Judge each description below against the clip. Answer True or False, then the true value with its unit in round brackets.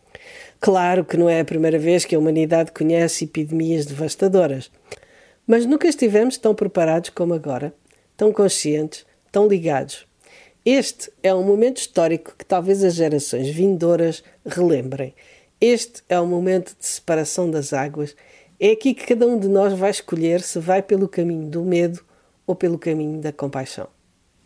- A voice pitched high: False (175 Hz)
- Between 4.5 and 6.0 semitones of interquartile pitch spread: False (3.9 semitones)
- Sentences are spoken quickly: False (155 wpm)